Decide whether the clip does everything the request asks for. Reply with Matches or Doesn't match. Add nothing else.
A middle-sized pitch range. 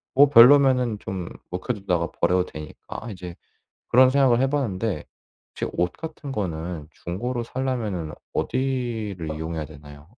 Doesn't match